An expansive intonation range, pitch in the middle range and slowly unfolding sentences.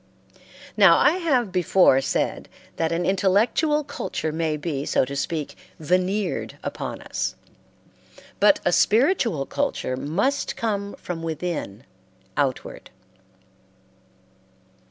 Yes: wide, 5.9 semitones; medium, 180 Hz; slow, 105 wpm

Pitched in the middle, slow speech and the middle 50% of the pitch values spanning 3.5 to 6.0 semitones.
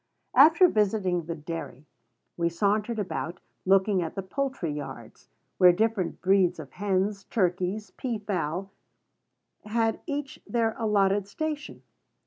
No: high, 200 Hz; slow, 120 wpm; average, 3.8 semitones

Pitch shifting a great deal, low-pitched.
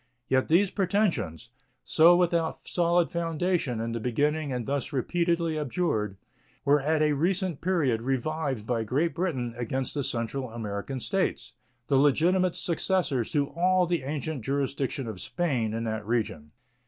No: wide, 6.0 semitones; medium, 145 Hz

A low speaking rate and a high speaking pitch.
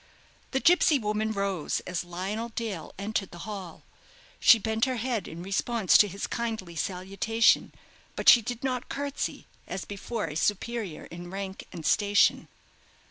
No: average, 150 wpm; high, 205 Hz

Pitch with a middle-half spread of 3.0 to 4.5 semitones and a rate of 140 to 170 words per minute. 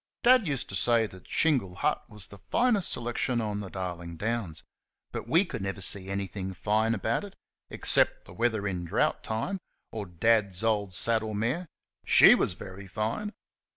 Yes: average, 3.8 semitones; average, 165 wpm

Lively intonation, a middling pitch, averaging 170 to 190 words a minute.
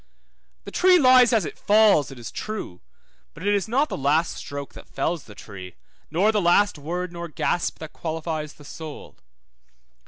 Yes: wide, 6.0 semitones; medium, 170 Hz; average, 180 wpm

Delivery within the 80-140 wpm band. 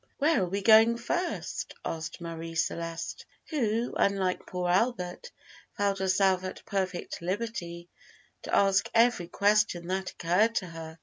Yes: slow, 135 wpm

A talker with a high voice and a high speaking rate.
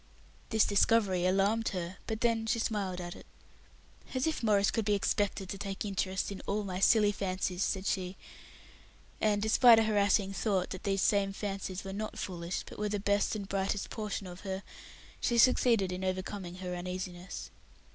No: high, 200 Hz; average, 175 wpm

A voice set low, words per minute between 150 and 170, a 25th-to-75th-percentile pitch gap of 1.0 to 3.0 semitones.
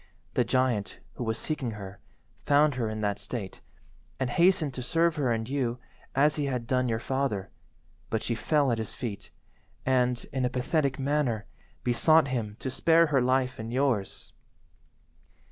No: low, 125 Hz; average, 165 wpm; average, 3.6 semitones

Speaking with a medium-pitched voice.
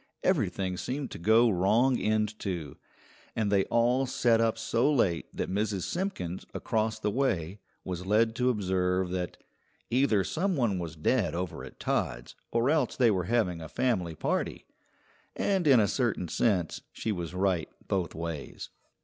No: low, 105 Hz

